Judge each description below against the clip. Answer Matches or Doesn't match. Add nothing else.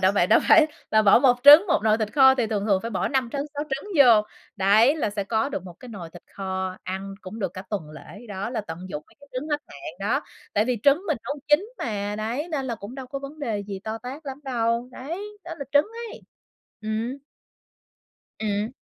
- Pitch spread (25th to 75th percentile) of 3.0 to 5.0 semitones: Doesn't match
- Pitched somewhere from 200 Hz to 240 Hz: Matches